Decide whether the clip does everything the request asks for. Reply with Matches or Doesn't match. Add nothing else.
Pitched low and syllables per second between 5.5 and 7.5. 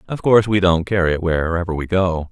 Matches